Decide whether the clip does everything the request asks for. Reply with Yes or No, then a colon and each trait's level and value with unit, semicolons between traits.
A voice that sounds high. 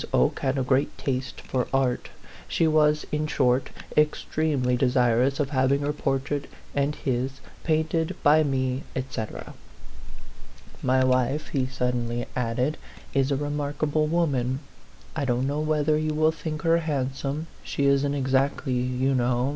No: low, 135 Hz